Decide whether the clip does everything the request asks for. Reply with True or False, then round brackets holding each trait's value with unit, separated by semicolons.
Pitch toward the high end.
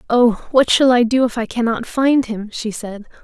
True (235 Hz)